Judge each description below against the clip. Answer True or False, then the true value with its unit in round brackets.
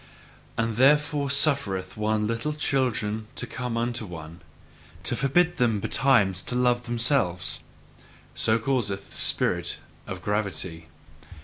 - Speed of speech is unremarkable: False (120 wpm)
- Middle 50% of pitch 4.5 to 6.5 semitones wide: True (5.2 semitones)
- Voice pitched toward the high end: False (115 Hz)